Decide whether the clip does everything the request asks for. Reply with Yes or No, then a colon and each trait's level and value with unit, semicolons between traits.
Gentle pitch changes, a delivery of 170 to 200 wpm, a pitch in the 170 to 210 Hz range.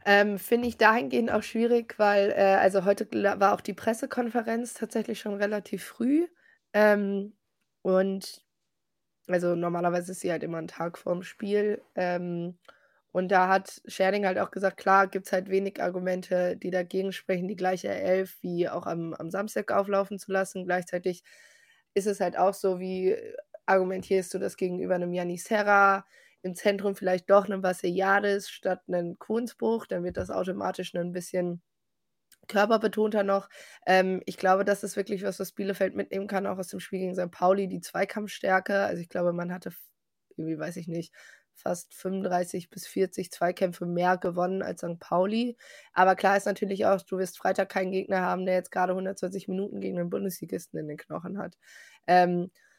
Yes: narrow, 1.9 semitones; average, 175 wpm; high, 190 Hz